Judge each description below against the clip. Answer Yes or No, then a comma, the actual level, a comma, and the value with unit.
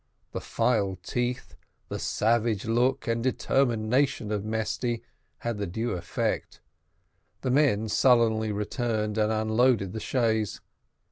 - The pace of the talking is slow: Yes, slow, 120 wpm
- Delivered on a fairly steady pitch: Yes, narrow, 2.3 semitones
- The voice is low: Yes, low, 110 Hz